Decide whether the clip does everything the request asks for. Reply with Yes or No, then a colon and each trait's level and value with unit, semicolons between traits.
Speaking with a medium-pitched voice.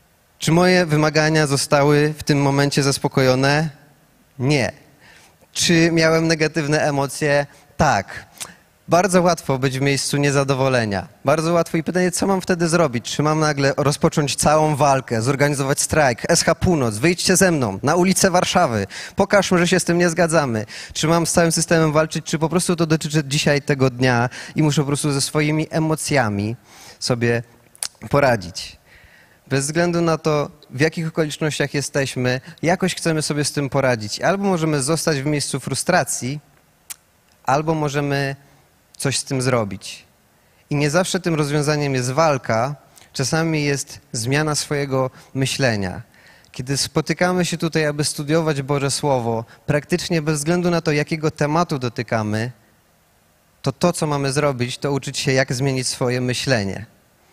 Yes: medium, 145 Hz